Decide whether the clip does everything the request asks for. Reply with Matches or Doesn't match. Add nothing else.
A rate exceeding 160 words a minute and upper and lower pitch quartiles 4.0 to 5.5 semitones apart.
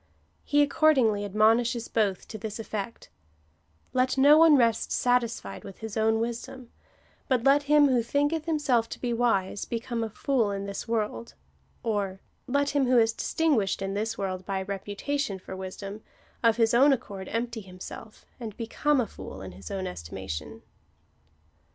Matches